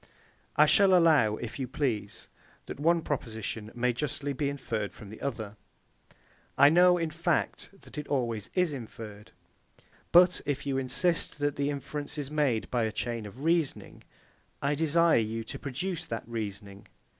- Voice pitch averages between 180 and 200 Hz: No, medium, 140 Hz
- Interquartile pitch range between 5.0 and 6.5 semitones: Yes, average, 5.3 semitones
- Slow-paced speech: No, average, 165 wpm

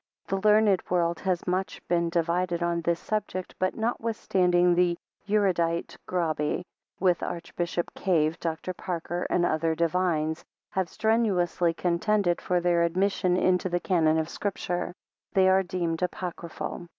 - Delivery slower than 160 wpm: Yes, slow, 135 wpm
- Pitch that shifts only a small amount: Yes, narrow, 1.6 semitones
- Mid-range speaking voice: Yes, medium, 175 Hz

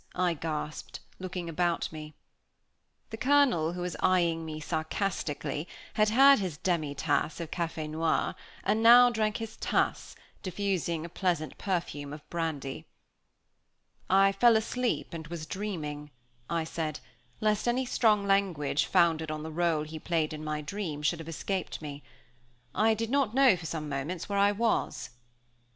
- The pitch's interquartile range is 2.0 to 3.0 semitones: No, average, 4.7 semitones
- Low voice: No, medium, 170 Hz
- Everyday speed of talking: Yes, average, 150 wpm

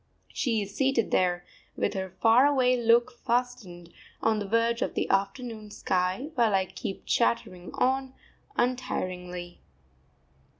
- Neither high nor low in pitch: No, high, 225 Hz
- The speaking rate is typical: No, slow, 130 wpm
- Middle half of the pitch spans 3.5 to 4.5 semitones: No, average, 4.9 semitones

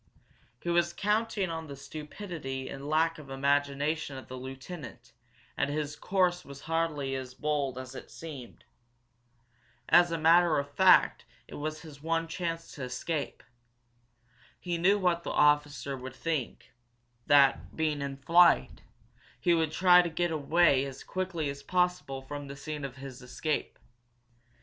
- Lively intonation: No, average, 3.6 semitones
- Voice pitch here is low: No, medium, 150 Hz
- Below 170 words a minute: Yes, average, 150 wpm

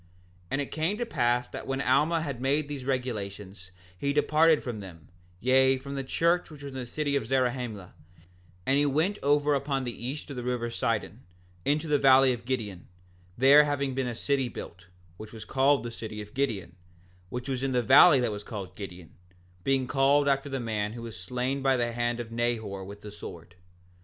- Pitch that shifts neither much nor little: Yes, average, 4.0 semitones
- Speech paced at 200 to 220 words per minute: Yes, fast, 205 wpm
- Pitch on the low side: Yes, low, 130 Hz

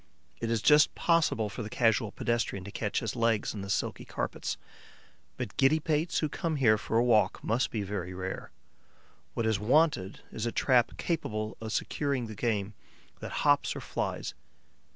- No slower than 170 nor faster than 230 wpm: Yes, average, 175 wpm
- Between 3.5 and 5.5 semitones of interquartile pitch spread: Yes, average, 4.2 semitones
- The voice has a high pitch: No, low, 115 Hz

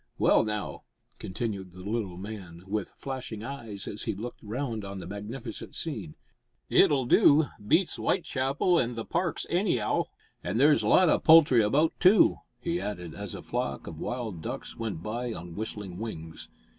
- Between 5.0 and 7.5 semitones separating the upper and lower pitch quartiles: Yes, wide, 5.5 semitones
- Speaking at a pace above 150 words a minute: Yes, average, 165 wpm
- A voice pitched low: Yes, low, 110 Hz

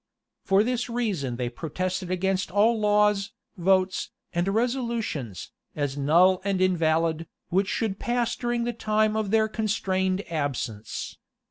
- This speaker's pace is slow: Yes, slow, 130 wpm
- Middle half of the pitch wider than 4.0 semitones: Yes, average, 4.5 semitones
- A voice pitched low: No, high, 190 Hz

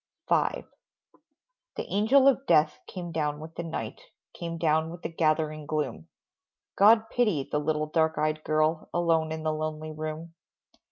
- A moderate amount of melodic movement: No, narrow, 1.7 semitones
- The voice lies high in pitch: No, medium, 160 Hz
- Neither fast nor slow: Yes, average, 155 wpm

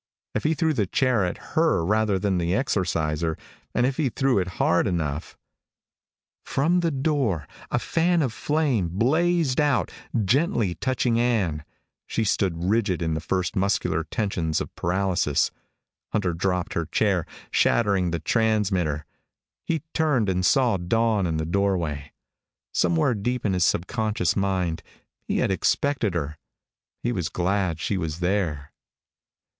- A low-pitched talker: Yes, low, 100 Hz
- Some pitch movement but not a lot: No, wide, 6.0 semitones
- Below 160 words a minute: Yes, average, 145 wpm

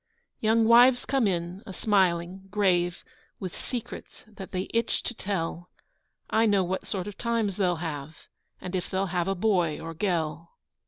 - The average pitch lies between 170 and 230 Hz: Yes, high, 190 Hz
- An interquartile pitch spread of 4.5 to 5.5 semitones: No, average, 3.5 semitones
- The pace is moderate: Yes, average, 165 wpm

